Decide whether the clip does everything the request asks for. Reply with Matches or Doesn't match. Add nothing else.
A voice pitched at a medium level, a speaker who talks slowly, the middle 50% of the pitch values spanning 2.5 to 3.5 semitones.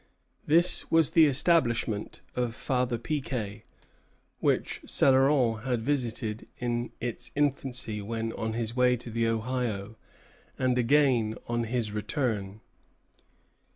Doesn't match